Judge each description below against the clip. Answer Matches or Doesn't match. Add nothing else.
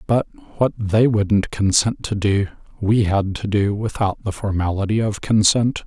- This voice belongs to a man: Matches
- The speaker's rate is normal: Matches